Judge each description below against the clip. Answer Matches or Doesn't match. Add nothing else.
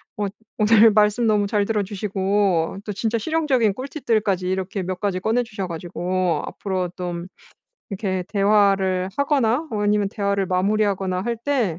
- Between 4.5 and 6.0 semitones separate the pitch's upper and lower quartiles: Doesn't match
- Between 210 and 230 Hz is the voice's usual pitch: Doesn't match